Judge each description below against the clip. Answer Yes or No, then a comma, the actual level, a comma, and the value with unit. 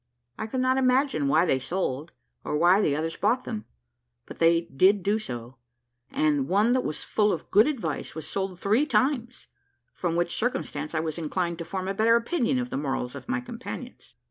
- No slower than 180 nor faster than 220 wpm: Yes, average, 195 wpm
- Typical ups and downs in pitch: No, wide, 6.9 semitones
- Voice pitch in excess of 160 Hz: Yes, high, 190 Hz